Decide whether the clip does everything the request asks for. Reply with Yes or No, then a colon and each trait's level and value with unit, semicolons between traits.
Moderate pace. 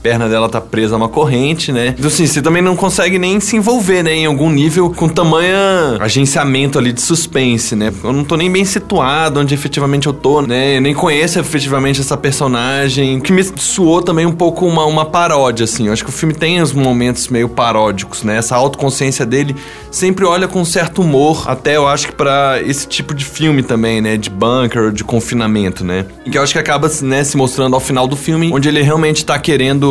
No: fast, 220 wpm